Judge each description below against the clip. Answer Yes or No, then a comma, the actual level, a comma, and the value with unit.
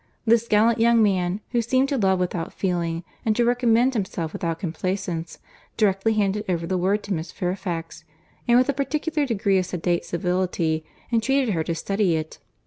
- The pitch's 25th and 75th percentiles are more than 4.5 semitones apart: Yes, average, 4.9 semitones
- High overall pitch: Yes, high, 195 Hz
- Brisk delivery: No, average, 175 wpm